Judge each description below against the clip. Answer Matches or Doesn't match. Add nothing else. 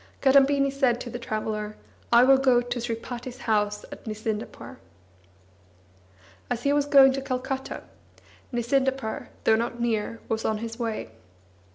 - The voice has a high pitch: Matches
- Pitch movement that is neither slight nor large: Matches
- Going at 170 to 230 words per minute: Doesn't match